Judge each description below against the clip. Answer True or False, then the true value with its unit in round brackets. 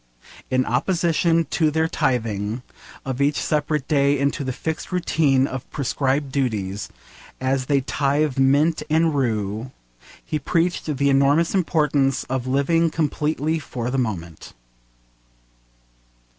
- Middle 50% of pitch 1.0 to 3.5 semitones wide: True (3.2 semitones)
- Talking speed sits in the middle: False (120 wpm)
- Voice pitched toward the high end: False (140 Hz)